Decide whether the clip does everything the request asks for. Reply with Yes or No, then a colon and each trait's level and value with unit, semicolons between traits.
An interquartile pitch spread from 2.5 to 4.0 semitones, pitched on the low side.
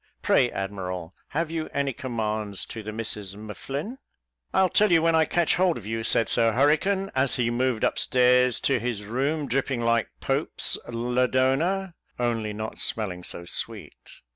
No: average, 5.3 semitones; low, 125 Hz